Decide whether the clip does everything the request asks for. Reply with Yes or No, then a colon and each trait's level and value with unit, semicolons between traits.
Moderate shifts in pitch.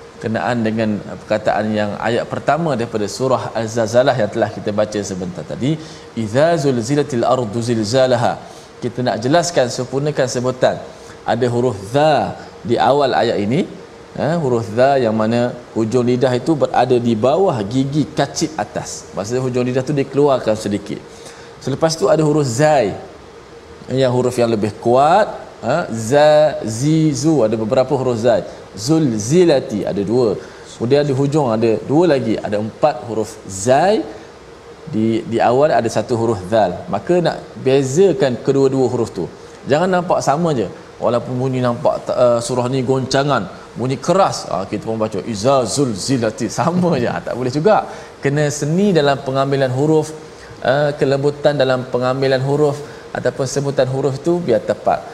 Yes: average, 4.0 semitones